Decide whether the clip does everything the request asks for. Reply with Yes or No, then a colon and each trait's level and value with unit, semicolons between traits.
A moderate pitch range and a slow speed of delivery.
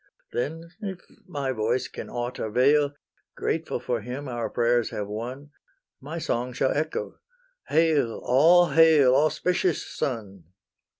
Yes: average, 4.7 semitones; slow, 125 wpm